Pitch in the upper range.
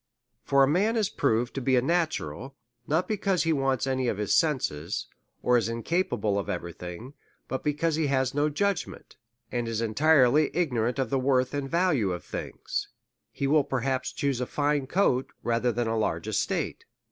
No: low, 135 Hz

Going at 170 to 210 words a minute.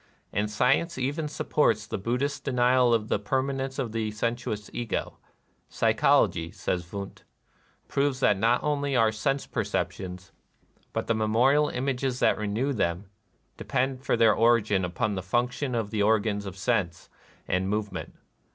No: average, 160 wpm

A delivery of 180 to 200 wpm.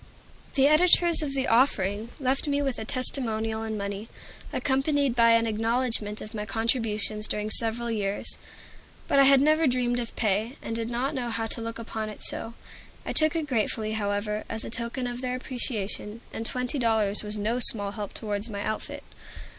Yes: average, 185 wpm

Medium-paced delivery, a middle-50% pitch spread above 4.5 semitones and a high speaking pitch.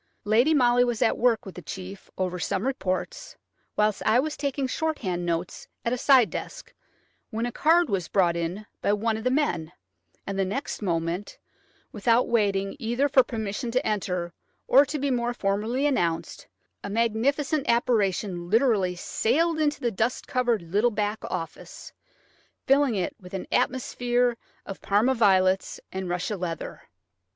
Yes: average, 160 wpm; average, 5.0 semitones; high, 220 Hz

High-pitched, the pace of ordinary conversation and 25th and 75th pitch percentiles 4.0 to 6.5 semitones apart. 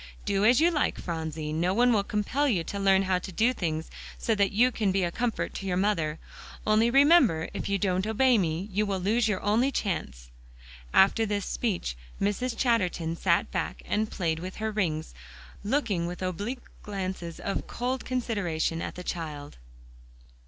Yes: high, 200 Hz; average, 180 wpm; average, 4.6 semitones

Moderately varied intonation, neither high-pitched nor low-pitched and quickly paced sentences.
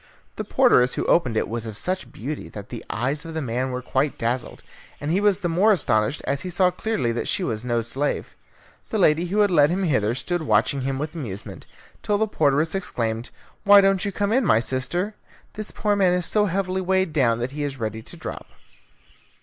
No: wide, 7.4 semitones; medium, 150 Hz; fast, 215 wpm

